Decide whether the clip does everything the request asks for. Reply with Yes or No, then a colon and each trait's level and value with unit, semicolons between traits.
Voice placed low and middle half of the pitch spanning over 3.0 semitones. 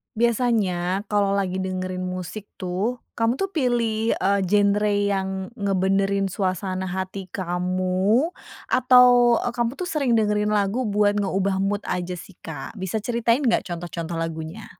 No: high, 200 Hz; average, 3.6 semitones